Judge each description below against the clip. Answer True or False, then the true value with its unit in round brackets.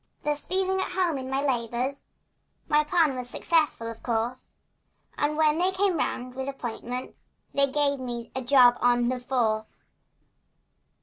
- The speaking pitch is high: True (265 Hz)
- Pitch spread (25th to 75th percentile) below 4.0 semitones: True (3.6 semitones)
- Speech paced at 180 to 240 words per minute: False (150 wpm)